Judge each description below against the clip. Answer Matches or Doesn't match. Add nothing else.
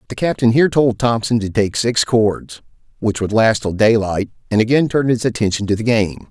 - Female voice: Doesn't match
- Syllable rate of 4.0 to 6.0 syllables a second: Matches